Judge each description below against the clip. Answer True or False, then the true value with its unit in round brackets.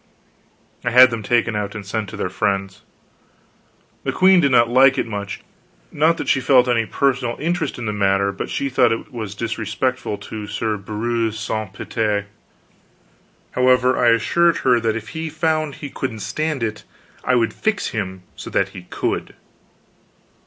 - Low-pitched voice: True (115 Hz)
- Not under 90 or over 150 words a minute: False (165 wpm)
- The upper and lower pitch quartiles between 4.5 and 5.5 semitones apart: False (3.9 semitones)